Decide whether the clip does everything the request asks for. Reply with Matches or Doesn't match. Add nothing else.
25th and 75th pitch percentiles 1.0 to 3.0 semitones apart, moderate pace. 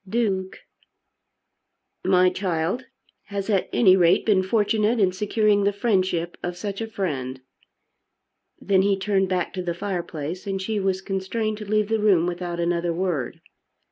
Matches